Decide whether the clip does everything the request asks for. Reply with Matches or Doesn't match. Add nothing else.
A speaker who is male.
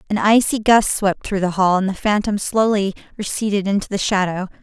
Doesn't match